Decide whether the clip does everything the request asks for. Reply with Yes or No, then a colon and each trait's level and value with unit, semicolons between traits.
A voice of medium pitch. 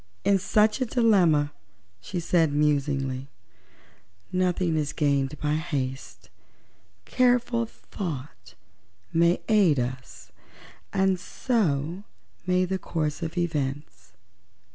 Yes: medium, 160 Hz